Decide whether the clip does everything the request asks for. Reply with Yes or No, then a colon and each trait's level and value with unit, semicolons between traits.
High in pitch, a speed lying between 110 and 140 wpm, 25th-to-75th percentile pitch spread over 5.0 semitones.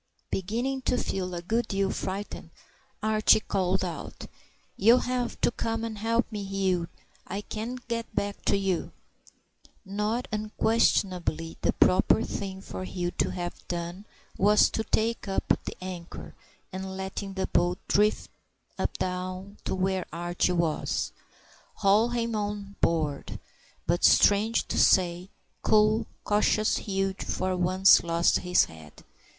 No: high, 195 Hz; slow, 135 wpm; average, 2.9 semitones